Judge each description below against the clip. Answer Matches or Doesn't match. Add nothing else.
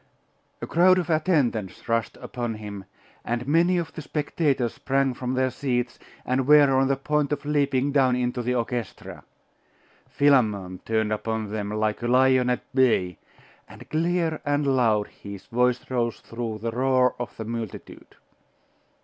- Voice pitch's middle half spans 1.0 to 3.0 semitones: Doesn't match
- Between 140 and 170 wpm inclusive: Matches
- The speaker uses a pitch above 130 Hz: Doesn't match